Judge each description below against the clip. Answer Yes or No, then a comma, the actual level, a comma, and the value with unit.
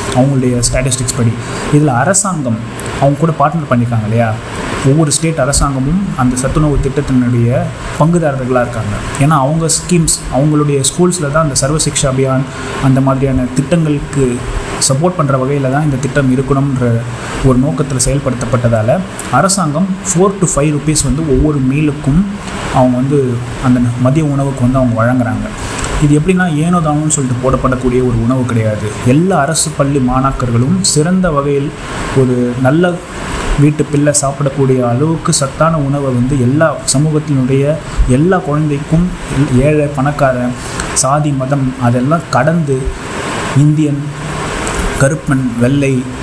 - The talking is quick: No, average, 120 wpm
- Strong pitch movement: No, average, 3.0 semitones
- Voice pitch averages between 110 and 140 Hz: Yes, low, 135 Hz